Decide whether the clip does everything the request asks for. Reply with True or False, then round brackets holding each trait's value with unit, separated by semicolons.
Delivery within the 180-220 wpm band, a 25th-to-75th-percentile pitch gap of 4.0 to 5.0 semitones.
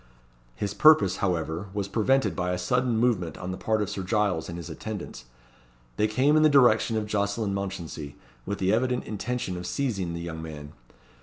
True (185 wpm; 4.3 semitones)